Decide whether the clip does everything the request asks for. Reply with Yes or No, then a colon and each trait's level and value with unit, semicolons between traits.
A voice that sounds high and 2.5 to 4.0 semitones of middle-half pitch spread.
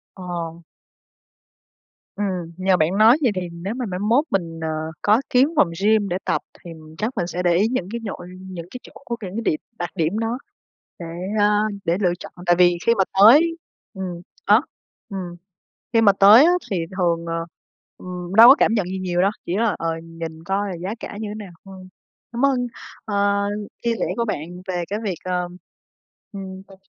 Yes: high, 195 Hz; average, 3.7 semitones